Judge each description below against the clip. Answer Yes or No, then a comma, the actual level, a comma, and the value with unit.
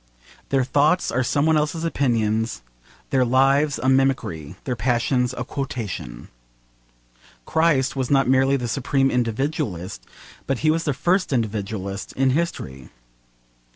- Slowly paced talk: Yes, slow, 130 wpm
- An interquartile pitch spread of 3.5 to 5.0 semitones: Yes, average, 3.9 semitones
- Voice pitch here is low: Yes, low, 130 Hz